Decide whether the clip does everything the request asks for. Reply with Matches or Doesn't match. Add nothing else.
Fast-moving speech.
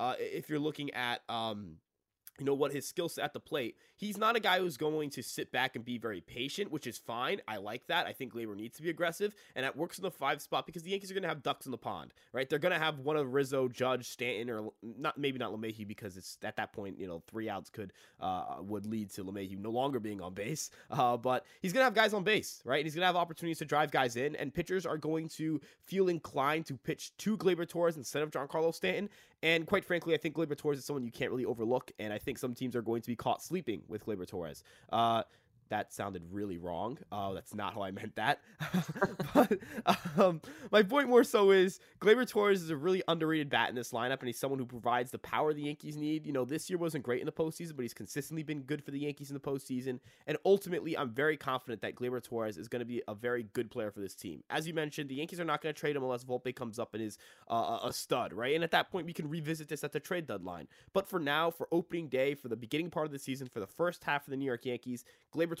Matches